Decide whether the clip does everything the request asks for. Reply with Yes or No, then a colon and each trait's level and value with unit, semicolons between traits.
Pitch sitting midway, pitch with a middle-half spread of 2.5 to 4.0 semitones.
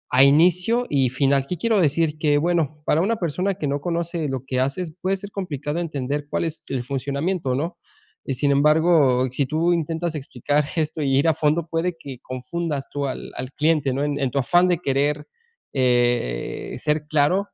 Yes: medium, 150 Hz; average, 3.7 semitones